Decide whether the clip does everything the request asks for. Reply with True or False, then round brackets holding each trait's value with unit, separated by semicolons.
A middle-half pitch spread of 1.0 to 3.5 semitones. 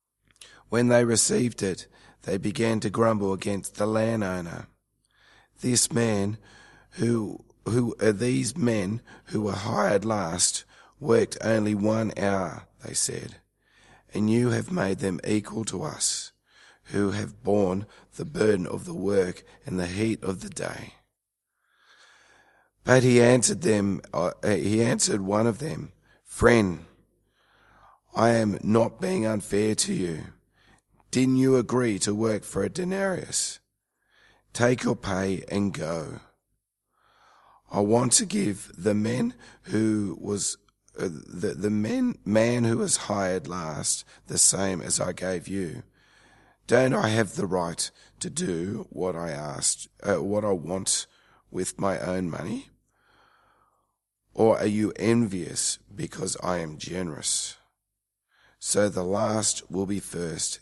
True (3.1 semitones)